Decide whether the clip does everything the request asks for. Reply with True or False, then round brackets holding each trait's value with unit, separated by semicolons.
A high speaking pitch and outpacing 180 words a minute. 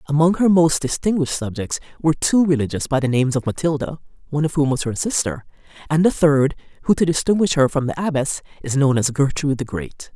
False (150 Hz; 205 wpm)